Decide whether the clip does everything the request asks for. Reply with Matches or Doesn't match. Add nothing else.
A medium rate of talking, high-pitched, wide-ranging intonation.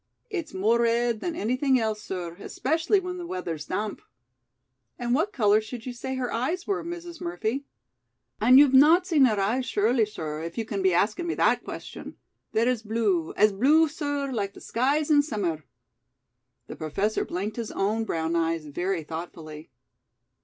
Matches